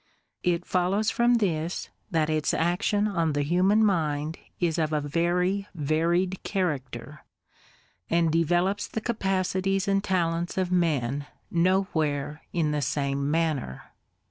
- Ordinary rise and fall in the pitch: Yes, average, 3.7 semitones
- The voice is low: No, medium, 170 Hz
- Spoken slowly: Yes, slow, 125 wpm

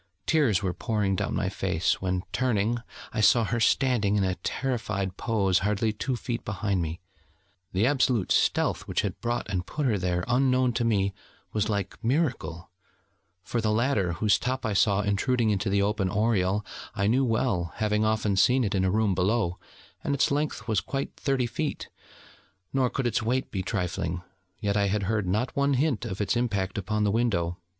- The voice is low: Yes, low, 105 Hz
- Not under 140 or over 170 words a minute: No, average, 185 wpm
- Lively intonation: No, average, 4.0 semitones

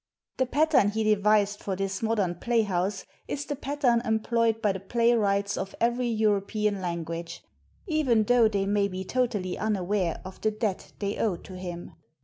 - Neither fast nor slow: Yes, average, 160 wpm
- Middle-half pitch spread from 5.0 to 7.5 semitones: No, average, 3.2 semitones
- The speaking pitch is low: No, high, 210 Hz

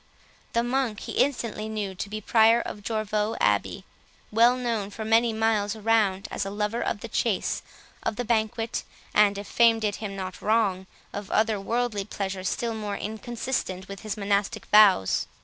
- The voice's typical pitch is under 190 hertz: No, high, 215 Hz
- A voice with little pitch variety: Yes, narrow, 2.0 semitones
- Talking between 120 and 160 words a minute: No, average, 175 wpm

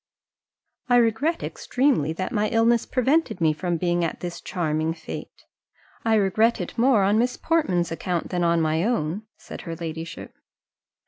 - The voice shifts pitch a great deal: Yes, wide, 5.9 semitones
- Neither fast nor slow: Yes, average, 155 wpm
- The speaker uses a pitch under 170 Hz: No, medium, 185 Hz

